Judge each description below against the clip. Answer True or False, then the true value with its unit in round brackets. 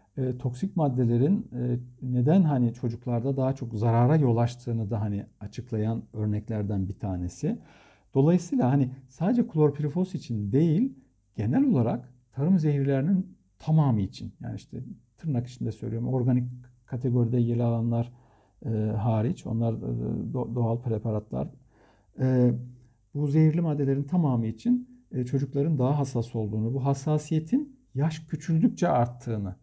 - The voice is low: True (125 Hz)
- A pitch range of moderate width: True (4.3 semitones)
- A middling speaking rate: True (125 wpm)